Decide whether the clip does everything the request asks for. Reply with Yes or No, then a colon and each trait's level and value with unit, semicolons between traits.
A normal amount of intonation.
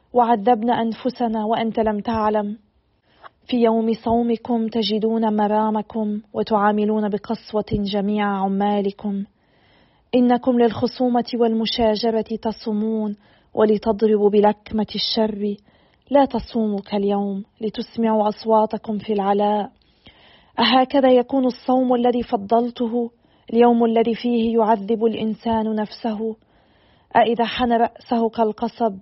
No: narrow, 1.8 semitones